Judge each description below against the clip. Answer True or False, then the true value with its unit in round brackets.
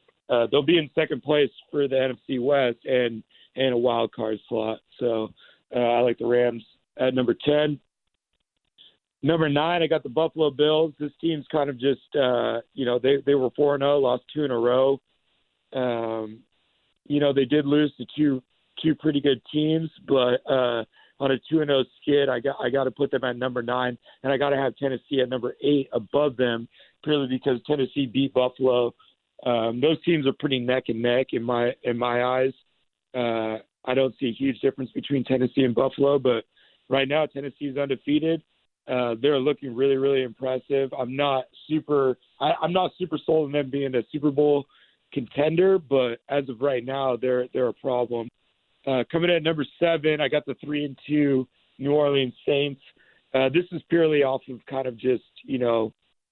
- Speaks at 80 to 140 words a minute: False (195 wpm)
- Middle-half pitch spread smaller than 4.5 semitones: True (2.8 semitones)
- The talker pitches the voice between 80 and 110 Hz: False (135 Hz)